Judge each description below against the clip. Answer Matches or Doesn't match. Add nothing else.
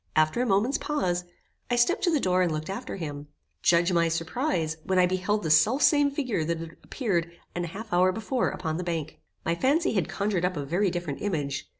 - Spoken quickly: Matches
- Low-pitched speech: Doesn't match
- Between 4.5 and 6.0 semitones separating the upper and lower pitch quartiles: Matches